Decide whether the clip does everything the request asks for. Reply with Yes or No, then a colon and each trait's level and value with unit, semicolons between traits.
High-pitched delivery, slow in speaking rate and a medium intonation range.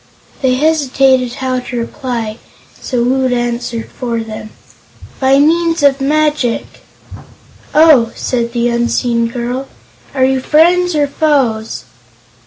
Yes: very high, 255 Hz; slow, 115 wpm; average, 3.3 semitones